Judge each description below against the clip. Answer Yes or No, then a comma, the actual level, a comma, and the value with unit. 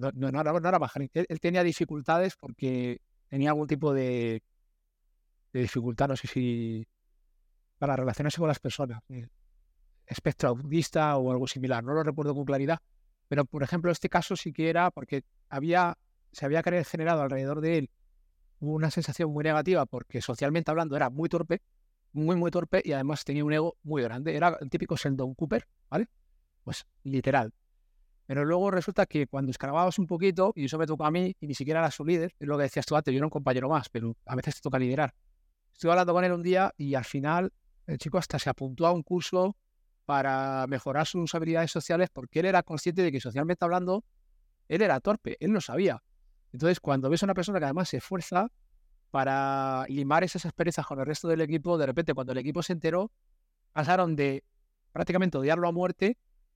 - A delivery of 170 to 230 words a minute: Yes, average, 195 wpm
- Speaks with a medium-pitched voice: Yes, medium, 150 Hz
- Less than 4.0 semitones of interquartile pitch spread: No, average, 4.5 semitones